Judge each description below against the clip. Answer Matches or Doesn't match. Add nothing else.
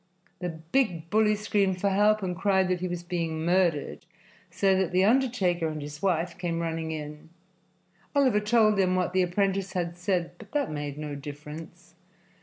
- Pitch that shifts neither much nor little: Matches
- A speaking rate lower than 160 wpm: Doesn't match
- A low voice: Doesn't match